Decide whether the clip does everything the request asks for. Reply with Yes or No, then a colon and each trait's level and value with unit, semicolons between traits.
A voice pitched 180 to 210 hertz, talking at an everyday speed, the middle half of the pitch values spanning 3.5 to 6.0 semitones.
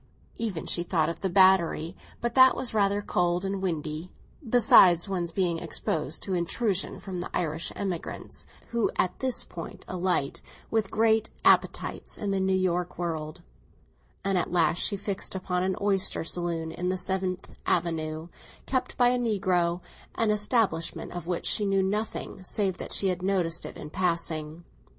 No: medium, 185 Hz; average, 160 wpm; average, 2.7 semitones